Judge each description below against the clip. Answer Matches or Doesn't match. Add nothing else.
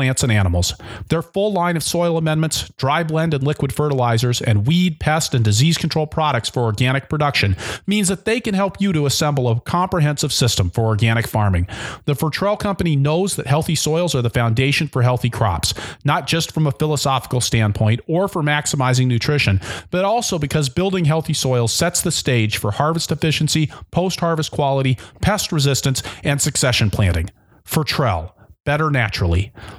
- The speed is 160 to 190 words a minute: Matches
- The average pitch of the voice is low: Doesn't match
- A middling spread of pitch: Doesn't match